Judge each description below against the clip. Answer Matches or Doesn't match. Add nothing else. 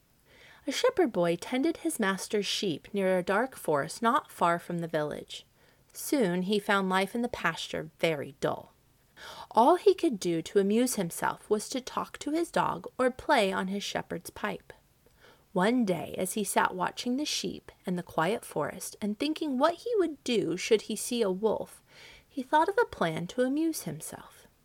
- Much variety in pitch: Matches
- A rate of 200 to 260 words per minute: Doesn't match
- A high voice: Matches